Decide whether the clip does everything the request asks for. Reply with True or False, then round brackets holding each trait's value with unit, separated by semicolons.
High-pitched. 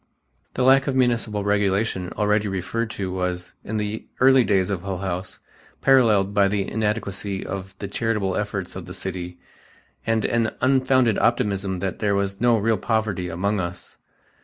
False (100 Hz)